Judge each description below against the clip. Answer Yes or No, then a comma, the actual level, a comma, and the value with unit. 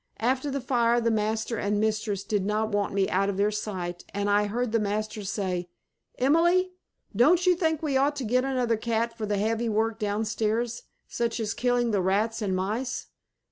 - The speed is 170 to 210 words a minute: Yes, average, 190 wpm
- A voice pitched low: No, high, 220 Hz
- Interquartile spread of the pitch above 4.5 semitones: No, average, 3.0 semitones